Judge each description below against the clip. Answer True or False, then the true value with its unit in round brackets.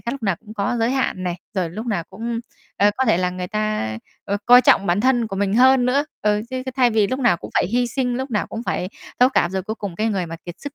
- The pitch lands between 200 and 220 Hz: True (215 Hz)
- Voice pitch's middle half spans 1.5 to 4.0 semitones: False (4.5 semitones)